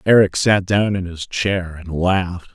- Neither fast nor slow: Yes, average, 190 wpm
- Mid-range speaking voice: No, very low, 95 Hz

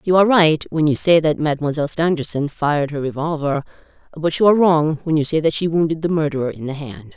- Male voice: No, female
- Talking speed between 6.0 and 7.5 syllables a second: Yes, 6.3 syllables/s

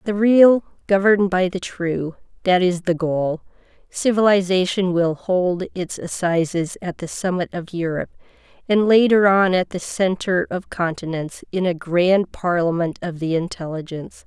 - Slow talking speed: No, average, 145 wpm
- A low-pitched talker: No, medium, 180 Hz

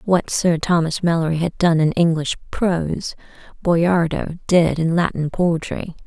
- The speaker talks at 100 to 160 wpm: Yes, average, 140 wpm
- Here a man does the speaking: No, female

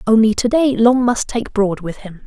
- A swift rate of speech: Yes, fast, 240 wpm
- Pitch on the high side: Yes, high, 225 Hz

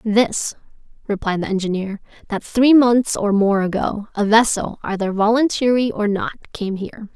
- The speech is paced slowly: No, average, 150 wpm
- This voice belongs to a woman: Yes, female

